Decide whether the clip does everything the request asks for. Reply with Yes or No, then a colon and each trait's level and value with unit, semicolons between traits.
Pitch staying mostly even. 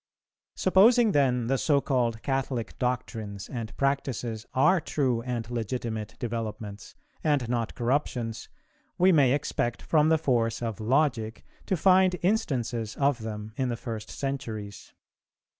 No: average, 4.0 semitones